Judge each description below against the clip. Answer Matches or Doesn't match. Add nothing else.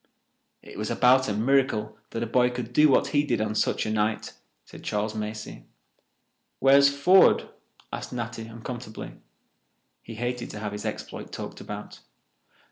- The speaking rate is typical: Matches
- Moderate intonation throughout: Matches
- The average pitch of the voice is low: Matches